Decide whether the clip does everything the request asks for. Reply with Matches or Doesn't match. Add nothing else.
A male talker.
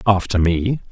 Matches